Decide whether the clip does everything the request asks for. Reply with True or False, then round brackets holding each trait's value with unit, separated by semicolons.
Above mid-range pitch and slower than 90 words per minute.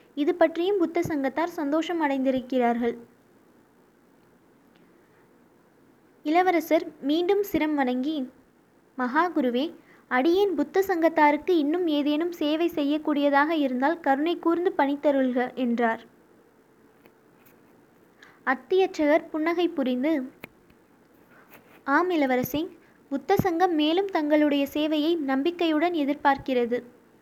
True (300 Hz; 80 wpm)